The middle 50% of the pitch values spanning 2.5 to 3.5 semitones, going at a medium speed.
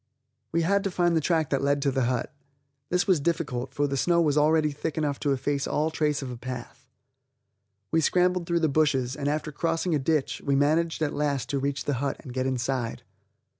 No: average, 3.1 semitones; fast, 215 wpm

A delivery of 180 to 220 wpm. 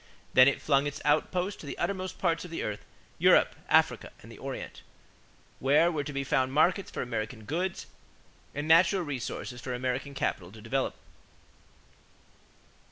No: average, 160 wpm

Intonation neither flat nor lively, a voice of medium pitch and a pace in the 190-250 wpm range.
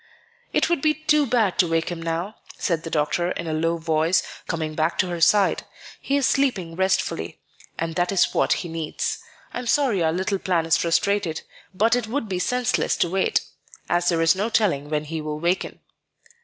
Yes: average, 4.4 semitones; medium, 175 Hz; average, 200 wpm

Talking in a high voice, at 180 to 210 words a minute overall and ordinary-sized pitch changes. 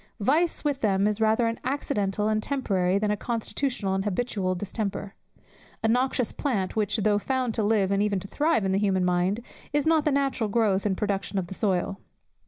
Yes: high, 210 Hz; average, 195 wpm; average, 4.0 semitones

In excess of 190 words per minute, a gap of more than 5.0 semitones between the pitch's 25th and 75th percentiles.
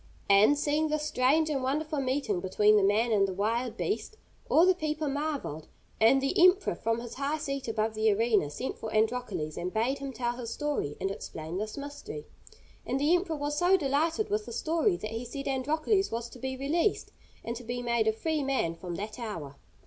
Yes: fast, 205 wpm; wide, 5.6 semitones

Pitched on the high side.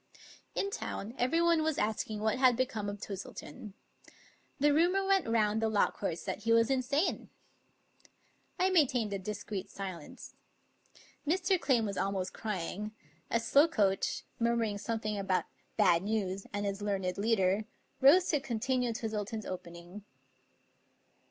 Yes: high, 220 Hz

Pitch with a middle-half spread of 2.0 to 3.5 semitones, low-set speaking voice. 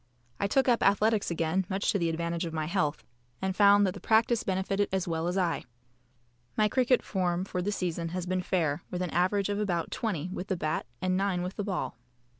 No: average, 2.9 semitones; medium, 185 Hz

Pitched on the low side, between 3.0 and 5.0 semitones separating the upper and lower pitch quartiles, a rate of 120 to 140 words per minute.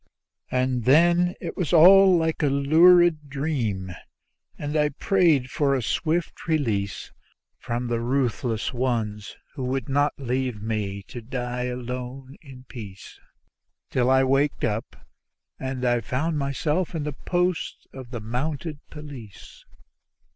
Yes: low, 130 Hz; average, 4.0 semitones; slow, 135 wpm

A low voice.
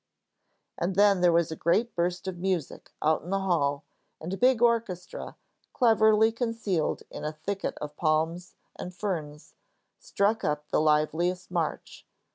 No: medium, 180 Hz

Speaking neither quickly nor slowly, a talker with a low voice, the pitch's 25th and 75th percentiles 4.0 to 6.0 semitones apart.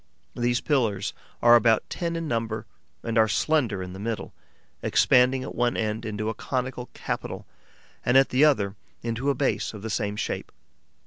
No: average, 175 wpm; low, 115 Hz; average, 3.3 semitones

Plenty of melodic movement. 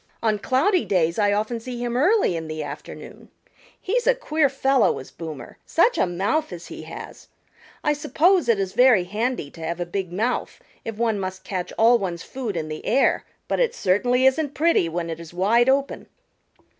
Yes: wide, 7.2 semitones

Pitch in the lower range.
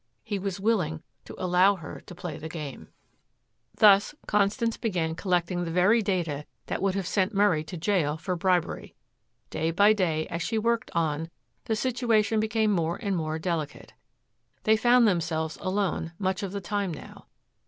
No: medium, 185 Hz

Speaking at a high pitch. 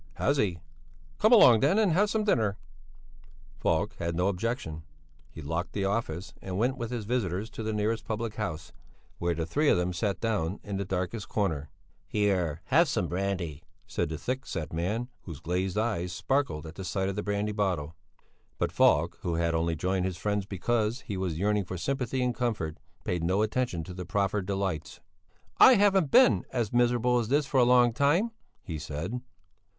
No: low, 100 Hz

